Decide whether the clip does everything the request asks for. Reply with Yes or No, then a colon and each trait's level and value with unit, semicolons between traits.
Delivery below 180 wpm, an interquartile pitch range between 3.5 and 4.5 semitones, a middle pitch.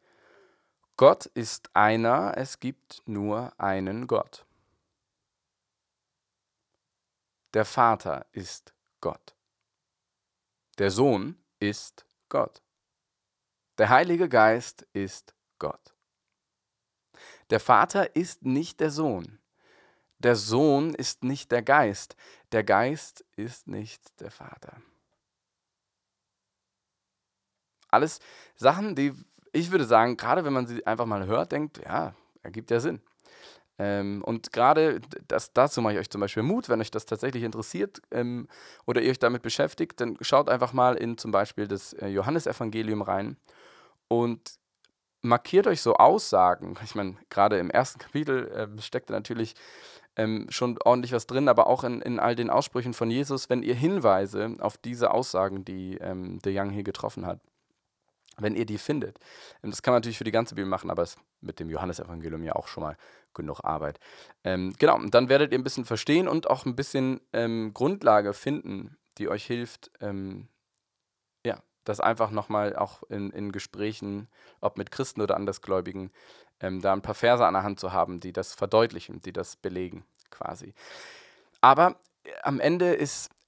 No: average, 150 wpm; average, 4.0 semitones; low, 110 Hz